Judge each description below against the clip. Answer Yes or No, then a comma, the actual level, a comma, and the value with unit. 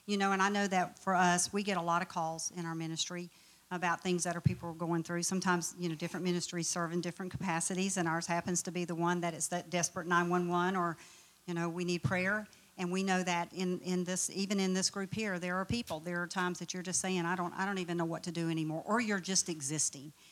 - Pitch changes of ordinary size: No, narrow, 1.5 semitones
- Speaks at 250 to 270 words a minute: Yes, fast, 260 wpm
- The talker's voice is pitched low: No, medium, 175 Hz